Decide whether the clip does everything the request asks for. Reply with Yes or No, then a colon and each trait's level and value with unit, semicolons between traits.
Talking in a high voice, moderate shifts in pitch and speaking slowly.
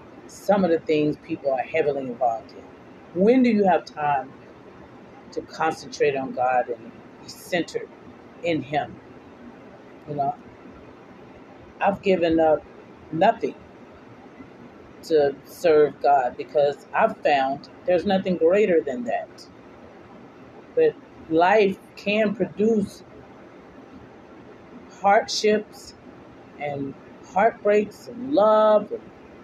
No: high, 195 Hz; wide, 5.9 semitones; slow, 100 wpm